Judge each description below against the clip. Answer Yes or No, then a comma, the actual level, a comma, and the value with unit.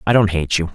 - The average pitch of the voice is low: Yes, very low, 95 Hz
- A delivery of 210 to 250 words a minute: No, fast, 320 wpm